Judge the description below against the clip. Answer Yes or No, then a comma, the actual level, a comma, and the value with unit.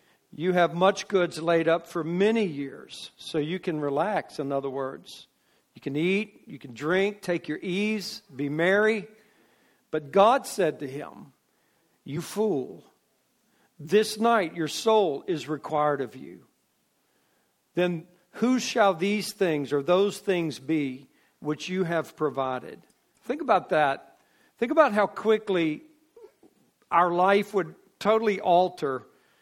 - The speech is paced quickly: No, slow, 135 wpm